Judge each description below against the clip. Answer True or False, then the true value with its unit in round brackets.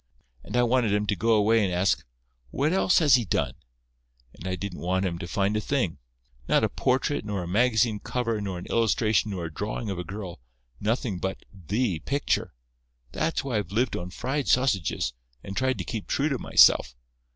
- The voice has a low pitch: True (105 Hz)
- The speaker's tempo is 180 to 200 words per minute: True (195 wpm)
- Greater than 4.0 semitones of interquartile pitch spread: True (5.1 semitones)